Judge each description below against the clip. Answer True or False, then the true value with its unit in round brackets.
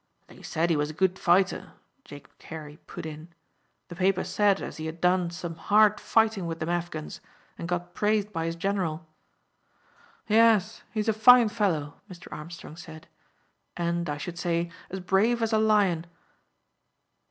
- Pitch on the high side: False (175 Hz)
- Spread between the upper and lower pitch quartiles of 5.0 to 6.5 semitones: False (4.0 semitones)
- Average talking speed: True (165 wpm)